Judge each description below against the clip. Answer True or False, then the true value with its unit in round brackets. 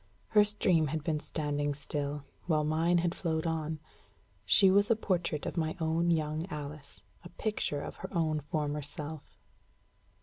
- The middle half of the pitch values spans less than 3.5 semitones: True (2.4 semitones)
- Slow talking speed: False (160 wpm)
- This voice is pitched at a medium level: True (155 Hz)